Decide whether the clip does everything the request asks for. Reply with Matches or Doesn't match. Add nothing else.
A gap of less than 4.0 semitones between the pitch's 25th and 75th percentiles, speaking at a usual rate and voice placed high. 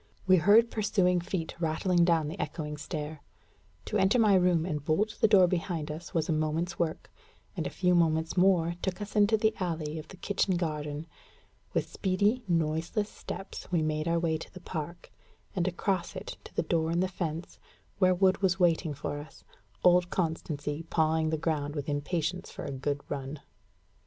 Doesn't match